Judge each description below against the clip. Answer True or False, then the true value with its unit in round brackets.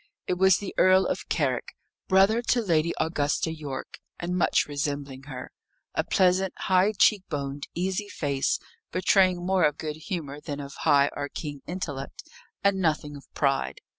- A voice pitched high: False (160 Hz)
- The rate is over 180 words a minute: False (160 wpm)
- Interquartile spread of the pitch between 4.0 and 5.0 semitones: True (4.7 semitones)